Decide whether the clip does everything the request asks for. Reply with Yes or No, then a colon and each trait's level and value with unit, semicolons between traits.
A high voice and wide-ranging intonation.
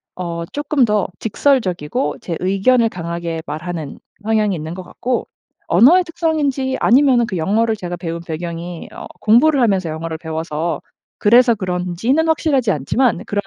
Yes: high, 195 Hz; wide, 7.0 semitones